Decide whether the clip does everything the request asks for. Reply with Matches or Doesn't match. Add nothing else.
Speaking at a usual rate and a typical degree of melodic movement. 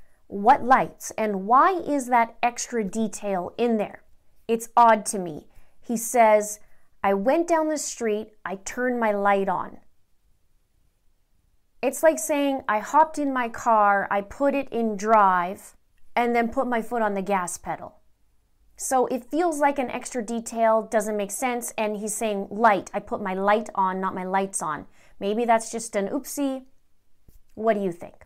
Matches